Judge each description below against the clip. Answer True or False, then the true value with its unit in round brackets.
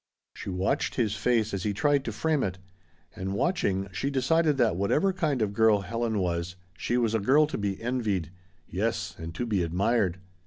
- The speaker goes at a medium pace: True (190 wpm)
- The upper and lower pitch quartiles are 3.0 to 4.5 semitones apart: False (4.9 semitones)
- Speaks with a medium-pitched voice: False (110 Hz)